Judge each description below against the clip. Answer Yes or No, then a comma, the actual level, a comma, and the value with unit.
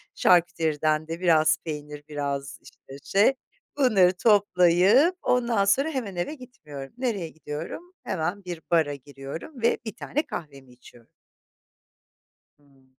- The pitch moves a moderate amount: No, wide, 6.0 semitones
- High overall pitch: No, medium, 170 Hz